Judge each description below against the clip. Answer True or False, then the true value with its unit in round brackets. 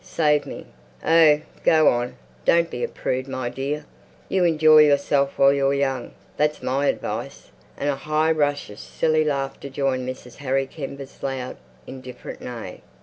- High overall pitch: False (140 Hz)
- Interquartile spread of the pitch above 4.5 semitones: False (2.5 semitones)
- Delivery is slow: False (155 wpm)